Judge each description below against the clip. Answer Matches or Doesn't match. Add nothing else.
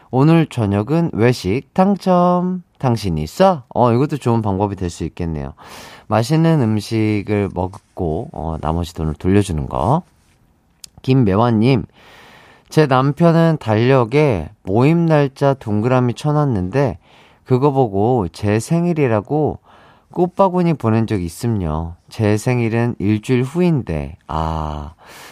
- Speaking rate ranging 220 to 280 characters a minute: Matches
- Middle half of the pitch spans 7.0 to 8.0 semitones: Matches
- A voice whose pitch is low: Matches